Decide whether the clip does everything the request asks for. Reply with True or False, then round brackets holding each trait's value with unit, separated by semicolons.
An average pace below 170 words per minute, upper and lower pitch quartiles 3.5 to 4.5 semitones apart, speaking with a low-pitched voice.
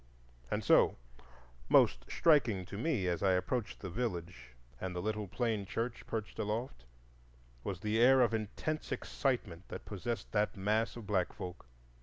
True (155 wpm; 4.1 semitones; 105 Hz)